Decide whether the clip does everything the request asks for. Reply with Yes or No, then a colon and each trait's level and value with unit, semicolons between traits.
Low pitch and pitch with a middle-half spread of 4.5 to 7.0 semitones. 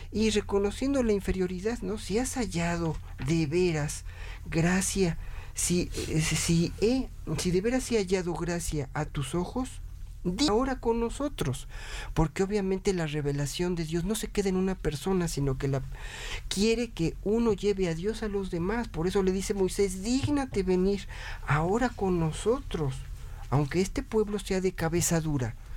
No: medium, 185 Hz; average, 5.0 semitones